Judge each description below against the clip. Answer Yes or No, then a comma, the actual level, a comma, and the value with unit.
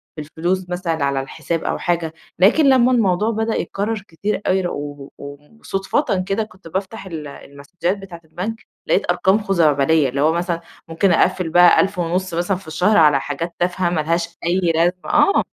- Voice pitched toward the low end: No, medium, 175 Hz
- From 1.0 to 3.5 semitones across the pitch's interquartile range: Yes, average, 3.2 semitones